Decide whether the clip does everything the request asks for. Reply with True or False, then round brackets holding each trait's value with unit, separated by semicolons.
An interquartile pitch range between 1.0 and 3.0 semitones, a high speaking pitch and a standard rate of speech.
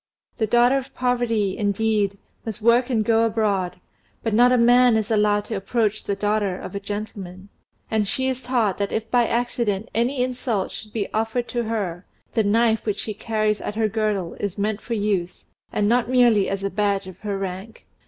True (2.7 semitones; 215 Hz; 195 wpm)